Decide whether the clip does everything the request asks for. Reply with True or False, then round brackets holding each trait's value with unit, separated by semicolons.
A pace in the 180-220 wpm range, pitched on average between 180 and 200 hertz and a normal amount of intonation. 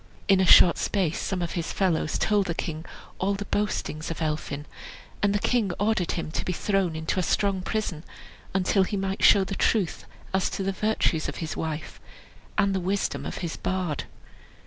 True (190 wpm; 190 Hz; 3.3 semitones)